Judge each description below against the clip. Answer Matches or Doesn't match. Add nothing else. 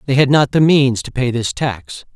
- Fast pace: Matches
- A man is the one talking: Matches